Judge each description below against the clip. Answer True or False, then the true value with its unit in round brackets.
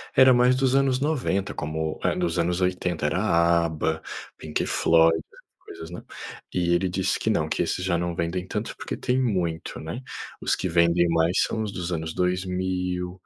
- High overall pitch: False (90 Hz)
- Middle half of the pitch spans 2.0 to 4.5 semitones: True (2.5 semitones)